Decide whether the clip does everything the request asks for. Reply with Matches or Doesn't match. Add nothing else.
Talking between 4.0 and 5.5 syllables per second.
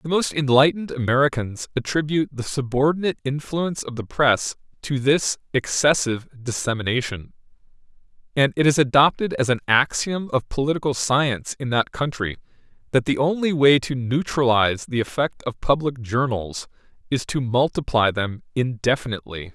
Matches